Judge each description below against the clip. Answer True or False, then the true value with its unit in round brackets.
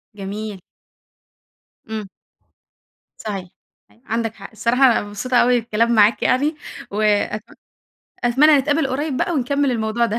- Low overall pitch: False (235 Hz)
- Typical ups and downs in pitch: True (3.5 semitones)